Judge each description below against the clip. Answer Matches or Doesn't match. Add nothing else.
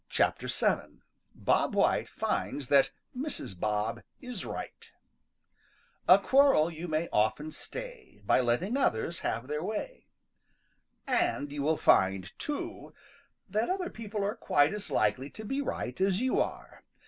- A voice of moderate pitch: Matches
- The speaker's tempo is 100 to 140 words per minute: Matches